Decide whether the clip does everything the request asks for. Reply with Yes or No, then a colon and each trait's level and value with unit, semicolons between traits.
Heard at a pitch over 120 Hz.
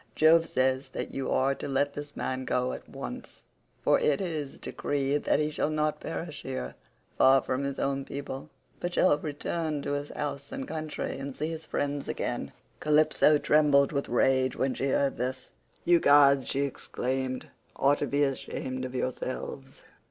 Yes: medium, 140 Hz